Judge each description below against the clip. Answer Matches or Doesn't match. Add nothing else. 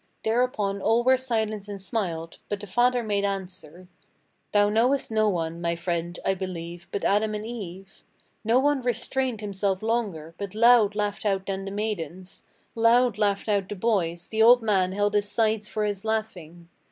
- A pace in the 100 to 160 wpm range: Doesn't match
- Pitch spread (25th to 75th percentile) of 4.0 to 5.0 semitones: Doesn't match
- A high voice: Matches